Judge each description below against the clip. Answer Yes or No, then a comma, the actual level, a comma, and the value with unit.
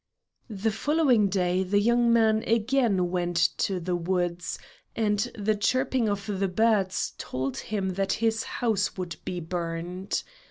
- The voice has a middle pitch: No, high, 195 Hz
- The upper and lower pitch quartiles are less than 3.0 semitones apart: No, average, 3.7 semitones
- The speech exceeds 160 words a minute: No, average, 145 wpm